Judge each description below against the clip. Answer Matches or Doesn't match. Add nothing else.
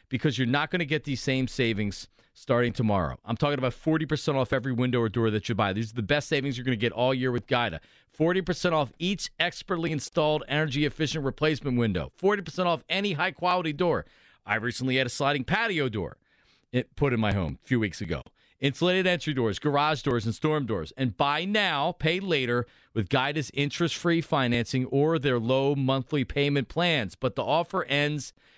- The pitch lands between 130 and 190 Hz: Matches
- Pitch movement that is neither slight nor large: Matches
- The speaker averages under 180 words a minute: Doesn't match